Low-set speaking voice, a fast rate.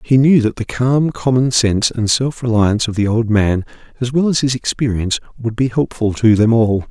Yes: low, 120 Hz; fast, 215 wpm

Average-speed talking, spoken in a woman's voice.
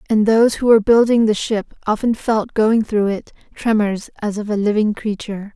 Yes: average, 195 wpm; female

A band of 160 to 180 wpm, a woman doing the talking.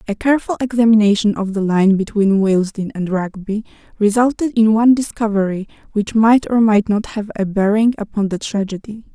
Yes: average, 165 wpm; female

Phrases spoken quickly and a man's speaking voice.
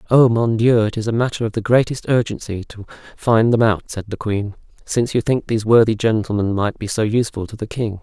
Yes: fast, 230 wpm; male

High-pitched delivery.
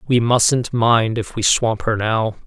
No: low, 115 Hz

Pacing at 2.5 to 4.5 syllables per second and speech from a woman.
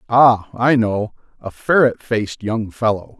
No: 4.1 syllables/s; male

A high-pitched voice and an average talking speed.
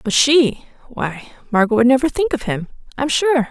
Yes: very high, 255 Hz; average, 170 wpm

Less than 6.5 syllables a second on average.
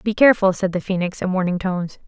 No: 6.6 syllables/s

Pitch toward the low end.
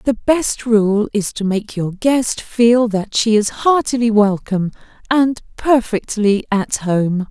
No: high, 220 Hz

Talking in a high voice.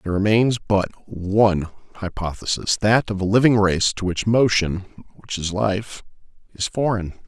No: low, 100 Hz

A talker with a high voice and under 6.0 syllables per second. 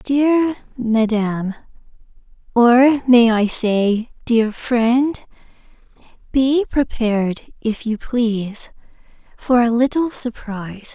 Yes: high, 240 Hz; 4.8 syllables/s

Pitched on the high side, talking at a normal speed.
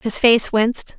Yes: high, 230 Hz; average, 185 wpm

